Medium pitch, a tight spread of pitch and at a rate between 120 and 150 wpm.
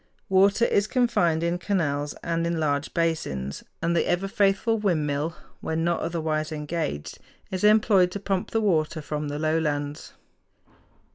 No: medium, 165 Hz; average, 4.2 semitones; average, 145 wpm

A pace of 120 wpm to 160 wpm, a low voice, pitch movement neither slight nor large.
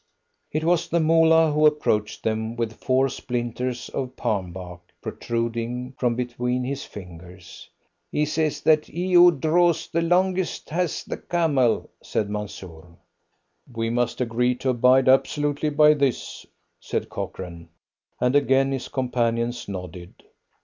Yes: slow, 135 wpm; low, 125 Hz; average, 5.0 semitones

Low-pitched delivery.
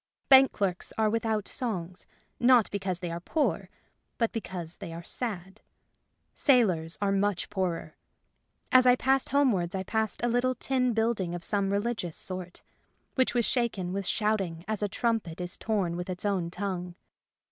No: high, 200 Hz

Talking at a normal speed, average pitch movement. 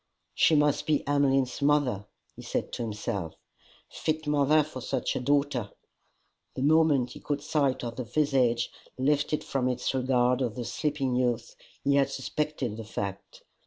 Yes: average, 160 wpm; average, 3.2 semitones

